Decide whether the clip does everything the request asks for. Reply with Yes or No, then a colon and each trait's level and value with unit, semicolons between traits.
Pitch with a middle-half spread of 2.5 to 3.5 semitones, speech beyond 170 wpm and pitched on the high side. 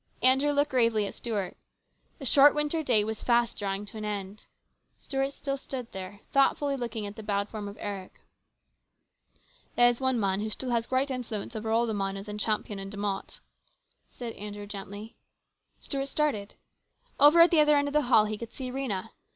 No: average, 4.7 semitones; average, 195 wpm; high, 225 Hz